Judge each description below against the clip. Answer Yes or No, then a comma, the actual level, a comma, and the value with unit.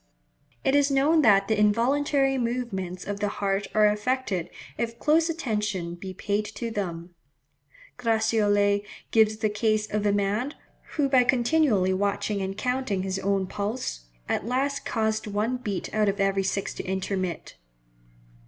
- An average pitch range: Yes, average, 3.9 semitones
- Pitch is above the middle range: Yes, high, 210 Hz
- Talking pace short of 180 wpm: Yes, average, 150 wpm